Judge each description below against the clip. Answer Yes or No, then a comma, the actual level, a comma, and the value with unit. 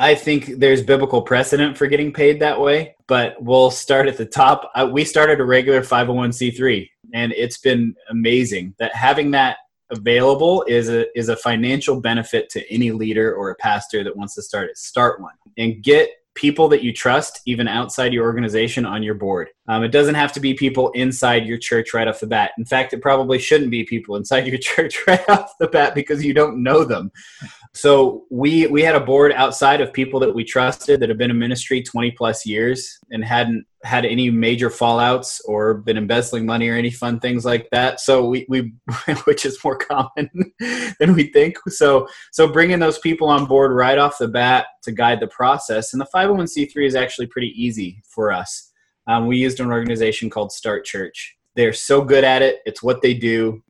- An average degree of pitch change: Yes, average, 3.4 semitones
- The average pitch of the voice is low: Yes, low, 125 Hz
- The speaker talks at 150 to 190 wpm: No, average, 200 wpm